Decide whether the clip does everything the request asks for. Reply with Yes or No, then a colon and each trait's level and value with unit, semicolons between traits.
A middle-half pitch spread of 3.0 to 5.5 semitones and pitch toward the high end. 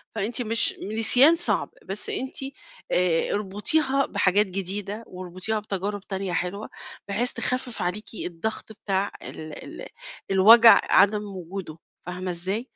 Yes: average, 3.4 semitones; high, 200 Hz